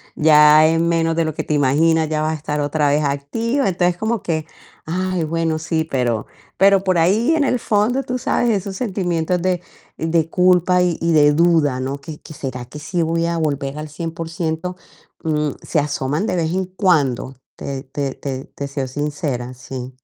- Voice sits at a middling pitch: Yes, medium, 160 Hz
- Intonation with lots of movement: No, average, 3.5 semitones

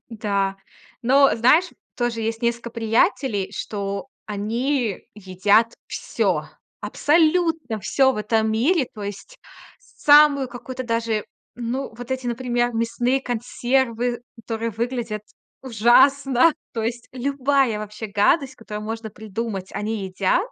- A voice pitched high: Yes, high, 235 Hz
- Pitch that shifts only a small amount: No, average, 3.3 semitones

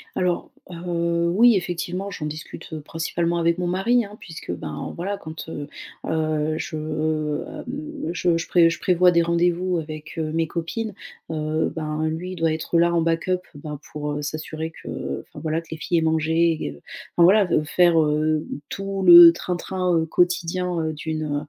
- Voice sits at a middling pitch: Yes, medium, 165 Hz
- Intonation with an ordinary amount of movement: No, narrow, 2.2 semitones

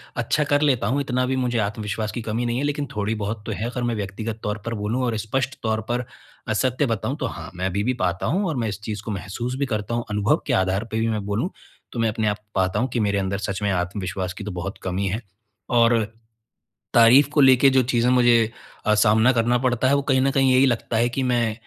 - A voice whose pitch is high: No, low, 115 Hz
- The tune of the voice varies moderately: Yes, average, 3.5 semitones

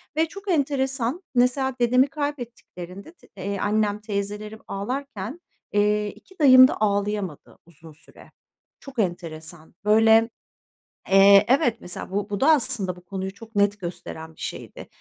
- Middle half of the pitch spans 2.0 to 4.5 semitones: No, average, 5.0 semitones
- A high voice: Yes, high, 210 Hz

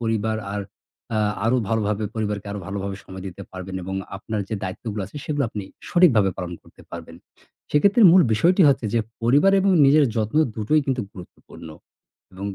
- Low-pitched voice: Yes, low, 110 Hz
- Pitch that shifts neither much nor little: No, wide, 5.9 semitones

